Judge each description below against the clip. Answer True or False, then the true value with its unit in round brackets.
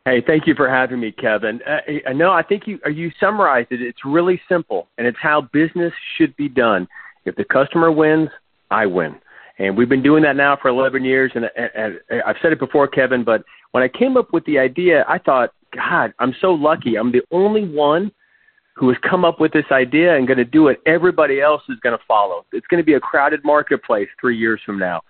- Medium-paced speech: False (230 wpm)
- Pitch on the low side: False (150 Hz)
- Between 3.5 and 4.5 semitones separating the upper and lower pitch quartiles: False (5.2 semitones)